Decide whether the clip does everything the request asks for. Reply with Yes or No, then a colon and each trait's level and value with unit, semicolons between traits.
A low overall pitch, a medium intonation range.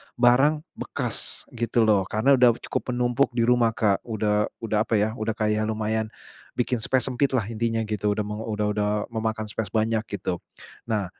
No: low, 110 Hz; narrow, 2.3 semitones